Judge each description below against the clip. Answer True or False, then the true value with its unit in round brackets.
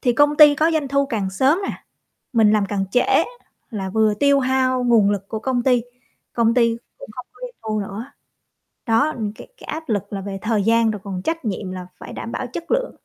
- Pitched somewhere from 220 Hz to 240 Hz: True (230 Hz)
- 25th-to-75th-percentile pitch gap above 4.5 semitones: True (5.0 semitones)